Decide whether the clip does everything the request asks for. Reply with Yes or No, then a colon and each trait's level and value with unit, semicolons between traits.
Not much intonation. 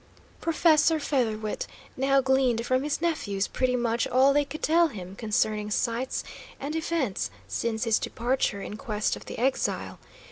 No: average, 4.3 semitones